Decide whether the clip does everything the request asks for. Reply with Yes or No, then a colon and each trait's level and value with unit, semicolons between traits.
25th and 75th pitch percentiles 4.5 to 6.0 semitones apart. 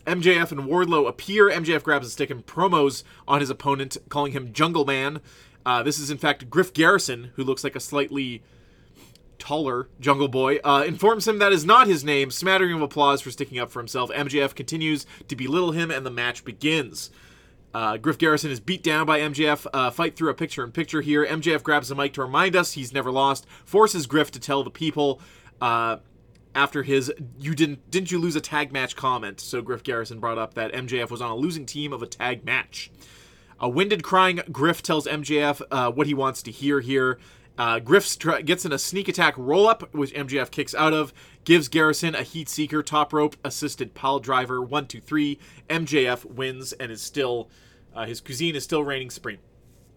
No: average, 3.4 semitones